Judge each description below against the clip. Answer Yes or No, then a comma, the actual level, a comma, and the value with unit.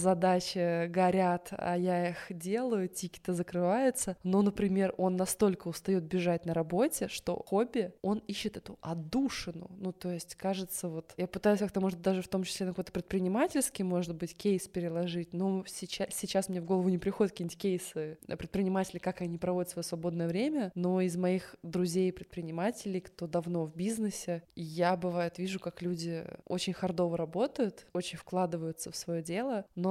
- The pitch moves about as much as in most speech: No, narrow, 1.7 semitones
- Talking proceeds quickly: Yes, fast, 165 wpm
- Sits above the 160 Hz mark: Yes, medium, 185 Hz